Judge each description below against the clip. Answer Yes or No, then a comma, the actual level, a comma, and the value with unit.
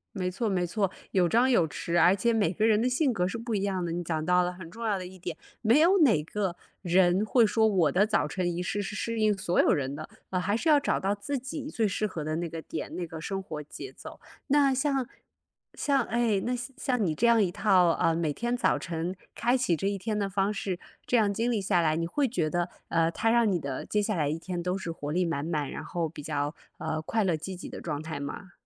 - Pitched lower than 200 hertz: Yes, high, 190 Hz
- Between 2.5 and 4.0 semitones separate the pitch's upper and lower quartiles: No, average, 5.0 semitones